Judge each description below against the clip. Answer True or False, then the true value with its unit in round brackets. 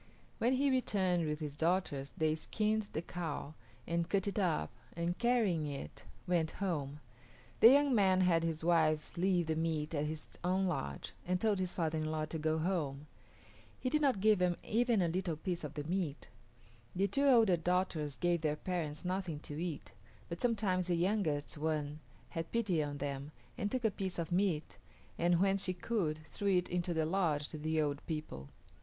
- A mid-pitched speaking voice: True (170 Hz)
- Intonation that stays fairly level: False (3.7 semitones)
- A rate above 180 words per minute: True (190 wpm)